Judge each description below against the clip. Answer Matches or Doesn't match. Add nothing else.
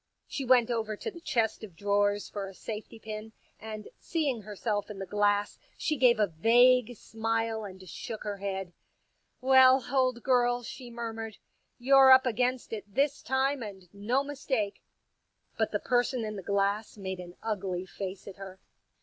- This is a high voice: Matches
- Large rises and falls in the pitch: Doesn't match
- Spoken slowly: Doesn't match